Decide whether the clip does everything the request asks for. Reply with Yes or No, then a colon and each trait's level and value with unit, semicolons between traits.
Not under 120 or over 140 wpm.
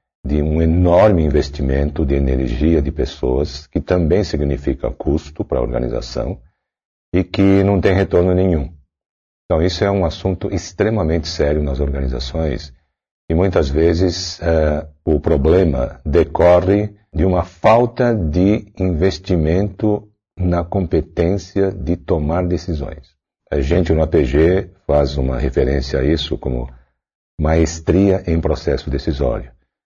Yes: average, 125 wpm